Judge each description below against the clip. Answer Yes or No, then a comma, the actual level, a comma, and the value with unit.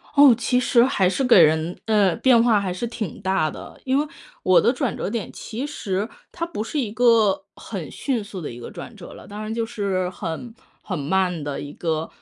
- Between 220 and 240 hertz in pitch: No, high, 205 Hz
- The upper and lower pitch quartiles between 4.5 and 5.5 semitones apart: Yes, average, 4.9 semitones